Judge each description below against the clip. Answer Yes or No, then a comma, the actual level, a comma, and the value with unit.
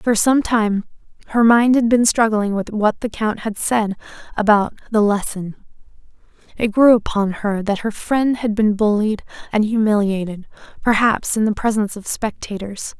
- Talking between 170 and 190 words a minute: No, average, 160 wpm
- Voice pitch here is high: Yes, high, 215 Hz